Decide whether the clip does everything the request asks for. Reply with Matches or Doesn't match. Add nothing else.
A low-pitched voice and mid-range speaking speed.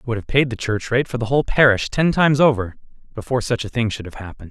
Doesn't match